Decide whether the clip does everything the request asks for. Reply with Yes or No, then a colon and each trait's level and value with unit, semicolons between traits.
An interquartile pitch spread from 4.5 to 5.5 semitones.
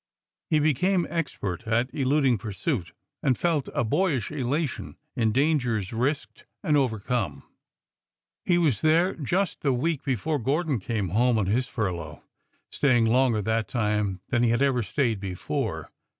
Yes: average, 5.2 semitones